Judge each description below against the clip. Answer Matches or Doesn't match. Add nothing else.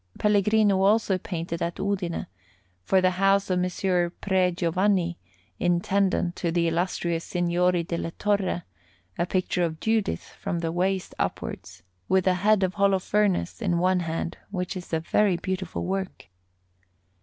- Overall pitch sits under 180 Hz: Doesn't match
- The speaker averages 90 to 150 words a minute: Matches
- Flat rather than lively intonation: Matches